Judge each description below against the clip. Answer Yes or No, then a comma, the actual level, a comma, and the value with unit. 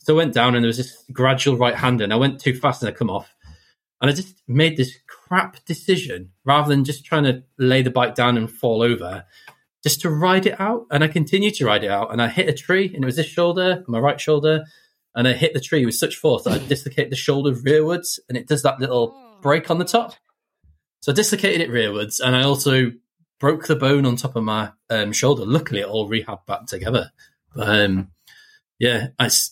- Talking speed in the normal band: No, fast, 230 wpm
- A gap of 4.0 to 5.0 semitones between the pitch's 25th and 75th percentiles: Yes, average, 4.7 semitones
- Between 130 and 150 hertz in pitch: Yes, low, 135 Hz